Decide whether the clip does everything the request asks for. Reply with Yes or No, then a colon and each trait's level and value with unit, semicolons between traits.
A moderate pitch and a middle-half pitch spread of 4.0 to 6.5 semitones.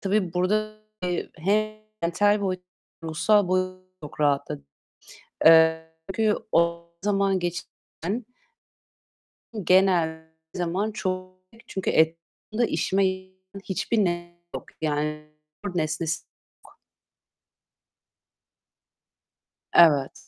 No: medium, 180 Hz; average, 3.3 semitones